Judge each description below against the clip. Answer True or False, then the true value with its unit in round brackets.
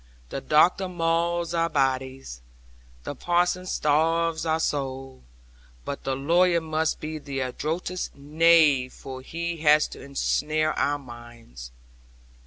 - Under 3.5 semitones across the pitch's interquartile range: False (3.8 semitones)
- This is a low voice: False (155 Hz)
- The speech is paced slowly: True (120 wpm)